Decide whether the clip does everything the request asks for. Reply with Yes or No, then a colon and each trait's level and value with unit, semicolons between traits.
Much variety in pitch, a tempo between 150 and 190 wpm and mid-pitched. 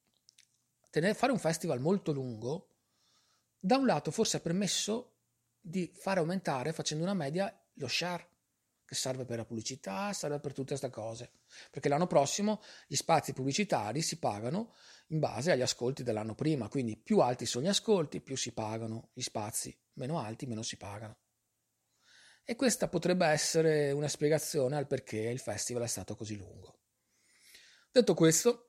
Yes: wide, 6.7 semitones; average, 155 wpm; medium, 145 Hz